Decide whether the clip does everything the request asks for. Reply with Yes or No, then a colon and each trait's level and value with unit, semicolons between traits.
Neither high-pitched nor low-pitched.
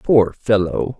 No: low, 110 Hz